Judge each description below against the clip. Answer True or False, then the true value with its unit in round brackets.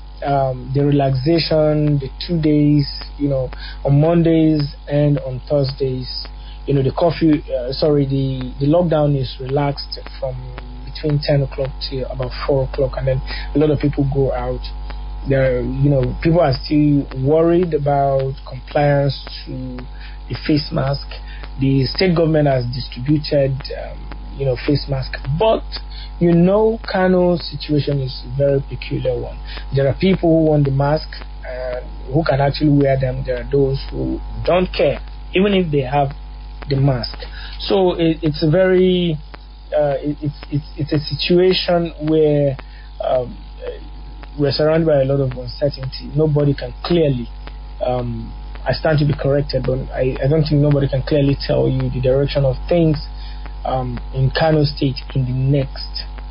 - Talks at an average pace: True (160 wpm)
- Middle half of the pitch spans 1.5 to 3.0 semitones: True (2.6 semitones)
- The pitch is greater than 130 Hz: True (140 Hz)